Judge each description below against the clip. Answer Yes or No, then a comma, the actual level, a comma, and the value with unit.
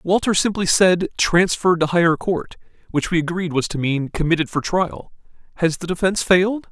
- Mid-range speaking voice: Yes, medium, 175 Hz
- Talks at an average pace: Yes, average, 180 wpm